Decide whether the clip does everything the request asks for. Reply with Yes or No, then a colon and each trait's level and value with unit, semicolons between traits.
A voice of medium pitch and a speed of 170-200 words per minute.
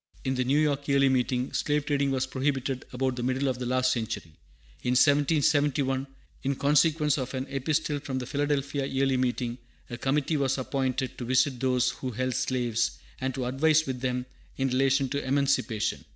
No: low, 130 Hz; average, 180 wpm